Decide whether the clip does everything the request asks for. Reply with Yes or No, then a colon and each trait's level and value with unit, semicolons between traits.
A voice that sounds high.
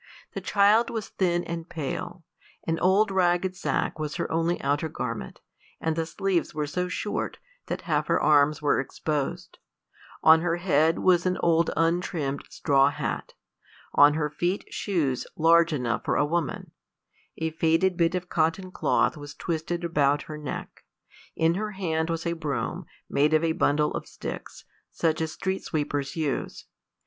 No: medium, 165 Hz